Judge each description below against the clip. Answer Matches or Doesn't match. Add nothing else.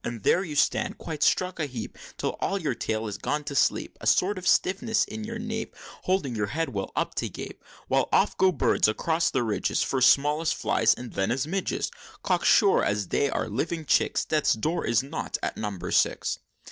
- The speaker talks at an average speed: Doesn't match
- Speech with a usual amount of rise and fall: Doesn't match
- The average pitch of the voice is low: Doesn't match